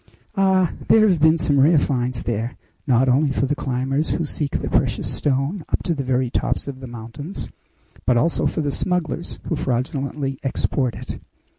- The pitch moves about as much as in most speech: Yes, average, 3.7 semitones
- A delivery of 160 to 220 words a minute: Yes, average, 180 wpm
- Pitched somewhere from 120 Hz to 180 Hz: Yes, medium, 140 Hz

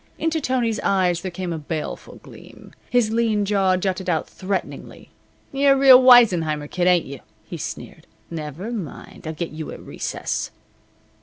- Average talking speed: Yes, average, 160 wpm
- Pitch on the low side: No, high, 190 Hz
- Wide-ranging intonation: Yes, wide, 5.9 semitones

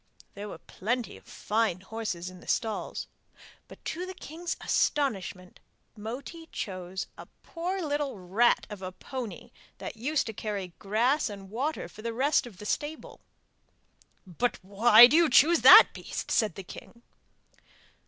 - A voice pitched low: No, high, 225 Hz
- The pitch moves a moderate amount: No, wide, 6.7 semitones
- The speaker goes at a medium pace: Yes, average, 155 wpm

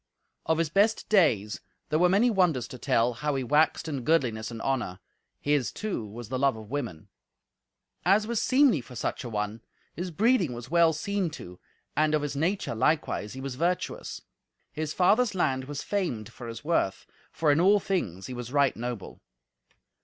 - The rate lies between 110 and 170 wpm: No, average, 185 wpm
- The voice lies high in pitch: No, medium, 145 Hz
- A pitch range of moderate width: No, wide, 6.9 semitones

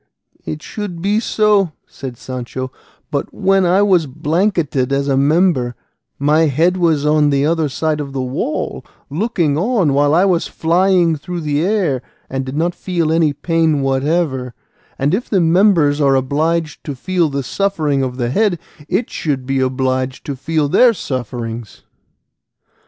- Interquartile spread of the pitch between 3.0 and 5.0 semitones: Yes, average, 4.5 semitones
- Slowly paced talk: No, average, 160 wpm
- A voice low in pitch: No, medium, 155 Hz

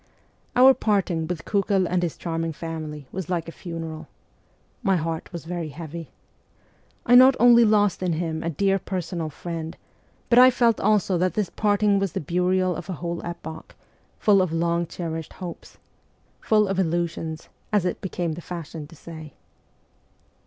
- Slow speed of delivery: No, average, 165 wpm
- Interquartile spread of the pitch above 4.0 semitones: No, average, 3.2 semitones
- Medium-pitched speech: Yes, medium, 175 Hz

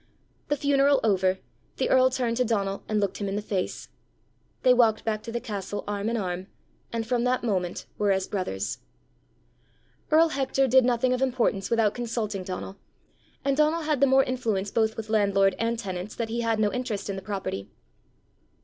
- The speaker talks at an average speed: Yes, average, 185 wpm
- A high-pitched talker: Yes, high, 225 Hz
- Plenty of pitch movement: No, average, 4.1 semitones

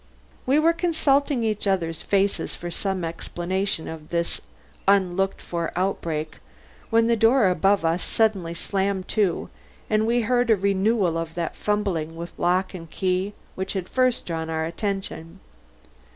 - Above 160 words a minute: No, average, 150 wpm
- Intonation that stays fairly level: No, average, 4.0 semitones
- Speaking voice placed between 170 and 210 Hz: Yes, high, 190 Hz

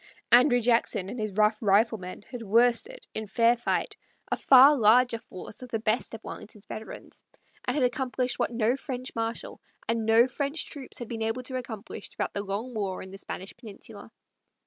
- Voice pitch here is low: No, high, 230 Hz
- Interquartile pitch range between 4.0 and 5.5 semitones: No, average, 2.7 semitones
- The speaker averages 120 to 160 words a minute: No, average, 185 wpm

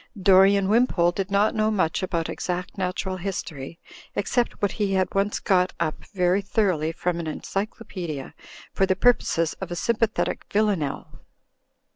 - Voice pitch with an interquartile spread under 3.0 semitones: Yes, narrow, 2.6 semitones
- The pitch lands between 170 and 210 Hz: Yes, high, 190 Hz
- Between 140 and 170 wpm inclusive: Yes, average, 145 wpm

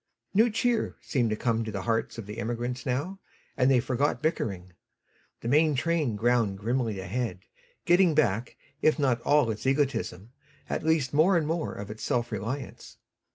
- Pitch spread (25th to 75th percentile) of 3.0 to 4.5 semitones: No, average, 5.3 semitones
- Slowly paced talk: No, average, 170 wpm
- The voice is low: Yes, low, 125 Hz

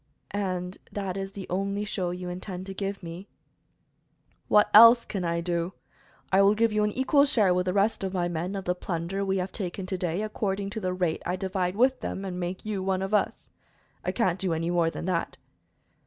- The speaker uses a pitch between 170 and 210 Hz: Yes, high, 190 Hz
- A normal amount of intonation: No, narrow, 2.1 semitones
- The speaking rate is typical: No, fast, 215 wpm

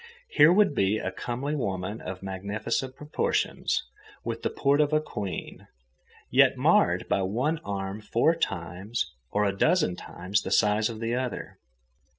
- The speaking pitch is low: Yes, low, 110 Hz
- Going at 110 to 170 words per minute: Yes, average, 145 wpm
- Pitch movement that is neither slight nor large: No, wide, 5.9 semitones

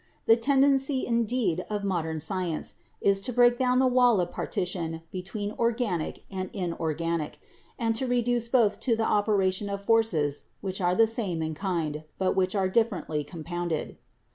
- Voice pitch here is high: Yes, high, 200 Hz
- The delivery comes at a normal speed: Yes, average, 160 wpm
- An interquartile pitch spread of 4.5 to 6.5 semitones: Yes, average, 5.1 semitones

